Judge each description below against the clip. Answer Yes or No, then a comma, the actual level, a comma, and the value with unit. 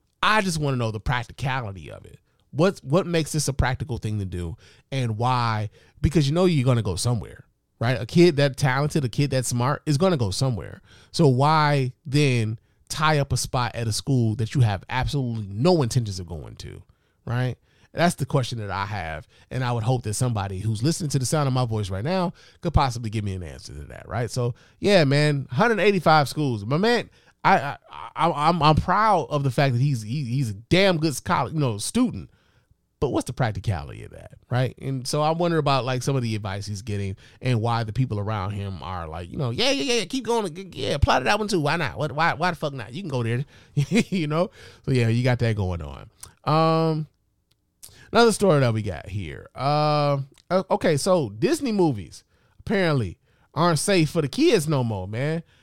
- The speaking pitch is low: Yes, low, 130 Hz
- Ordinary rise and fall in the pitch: No, wide, 6.1 semitones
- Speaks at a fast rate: Yes, fast, 215 wpm